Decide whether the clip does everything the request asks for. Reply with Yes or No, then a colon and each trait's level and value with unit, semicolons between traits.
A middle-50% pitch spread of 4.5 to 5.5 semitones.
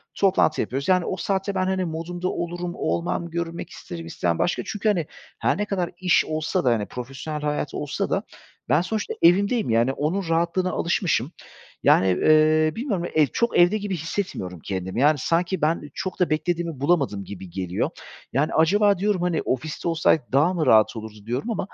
Yes: average, 5.1 semitones